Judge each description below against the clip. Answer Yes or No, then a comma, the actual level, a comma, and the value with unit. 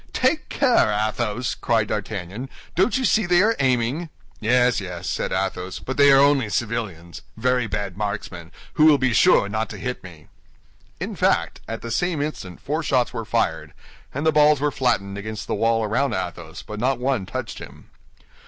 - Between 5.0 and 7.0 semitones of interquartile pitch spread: Yes, wide, 5.6 semitones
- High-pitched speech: No, low, 115 Hz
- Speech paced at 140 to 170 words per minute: No, average, 180 wpm